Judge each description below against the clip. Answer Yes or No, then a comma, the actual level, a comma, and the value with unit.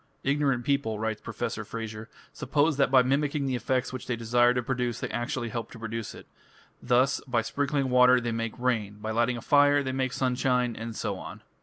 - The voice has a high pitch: No, low, 125 Hz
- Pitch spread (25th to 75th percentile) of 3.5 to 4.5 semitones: No, narrow, 2.6 semitones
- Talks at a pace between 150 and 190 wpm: No, average, 200 wpm